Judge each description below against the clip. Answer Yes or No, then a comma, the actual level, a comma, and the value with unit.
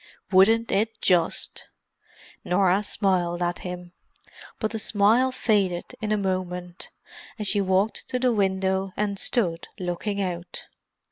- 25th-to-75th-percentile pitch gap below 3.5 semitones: Yes, average, 2.8 semitones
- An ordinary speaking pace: No, slow, 130 wpm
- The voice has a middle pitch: No, high, 195 Hz